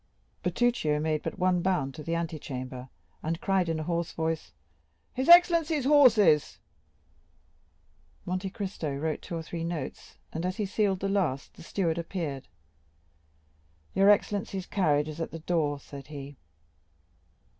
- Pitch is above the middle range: No, medium, 170 Hz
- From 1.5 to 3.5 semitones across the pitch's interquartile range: No, average, 4.2 semitones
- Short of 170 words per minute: Yes, average, 145 wpm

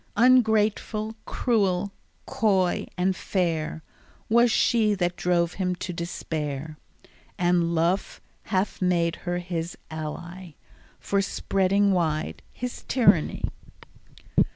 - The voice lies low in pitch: No, medium, 180 Hz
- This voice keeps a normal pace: No, slow, 100 wpm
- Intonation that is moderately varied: Yes, average, 3.2 semitones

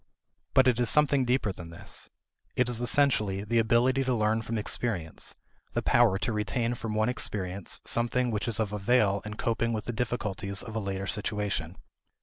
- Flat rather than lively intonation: No, average, 3.1 semitones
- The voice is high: No, low, 110 Hz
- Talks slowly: No, average, 180 wpm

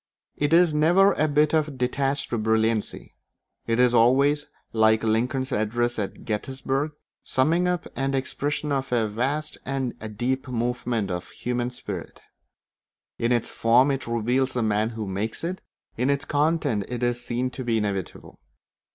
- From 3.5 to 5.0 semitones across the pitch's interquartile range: Yes, average, 3.8 semitones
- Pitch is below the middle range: Yes, low, 125 Hz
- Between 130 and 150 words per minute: No, average, 160 wpm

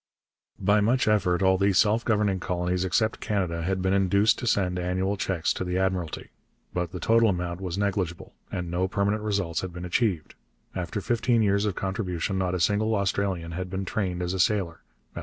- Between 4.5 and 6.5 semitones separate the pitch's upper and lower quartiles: No, narrow, 2.4 semitones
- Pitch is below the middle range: Yes, very low, 95 Hz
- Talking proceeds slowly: No, average, 190 wpm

